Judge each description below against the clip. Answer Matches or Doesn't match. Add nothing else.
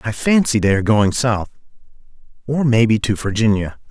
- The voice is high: Doesn't match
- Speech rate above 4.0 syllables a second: Matches